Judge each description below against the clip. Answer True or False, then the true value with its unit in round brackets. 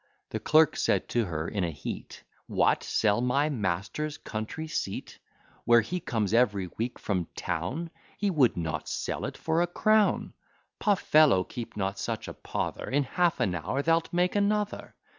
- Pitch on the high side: False (125 Hz)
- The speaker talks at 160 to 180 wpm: True (170 wpm)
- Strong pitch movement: True (8.9 semitones)